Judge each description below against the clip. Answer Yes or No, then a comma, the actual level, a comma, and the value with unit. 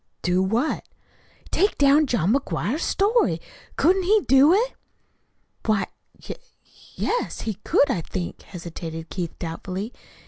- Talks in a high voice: Yes, high, 235 Hz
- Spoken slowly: Yes, slow, 125 wpm